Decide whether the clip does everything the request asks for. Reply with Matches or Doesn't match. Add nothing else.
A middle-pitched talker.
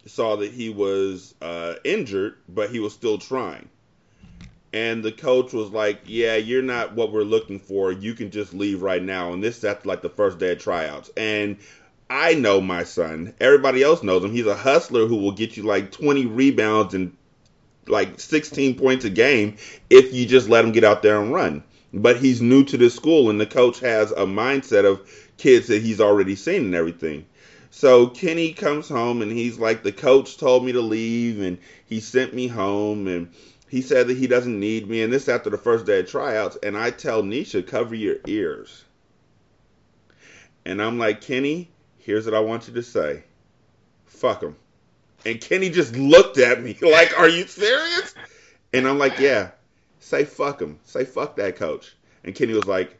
Doesn't match